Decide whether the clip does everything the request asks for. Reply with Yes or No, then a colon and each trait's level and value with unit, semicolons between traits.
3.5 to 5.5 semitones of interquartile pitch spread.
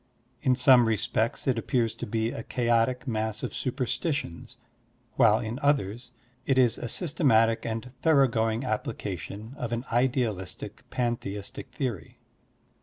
No: narrow, 2.5 semitones